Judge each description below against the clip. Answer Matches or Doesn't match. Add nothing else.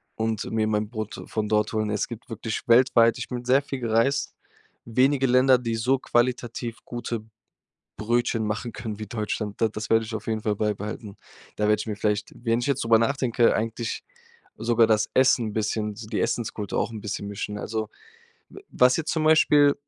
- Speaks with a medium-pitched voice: Doesn't match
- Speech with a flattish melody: Matches